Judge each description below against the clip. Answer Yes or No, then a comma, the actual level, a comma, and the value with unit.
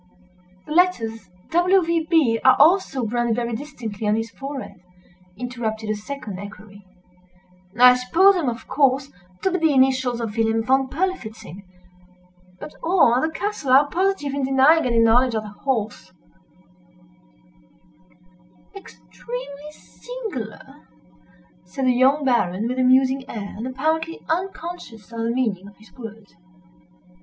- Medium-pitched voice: No, very high, 255 Hz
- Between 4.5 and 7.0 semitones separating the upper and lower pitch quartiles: Yes, average, 5.1 semitones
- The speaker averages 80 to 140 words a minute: Yes, slow, 135 wpm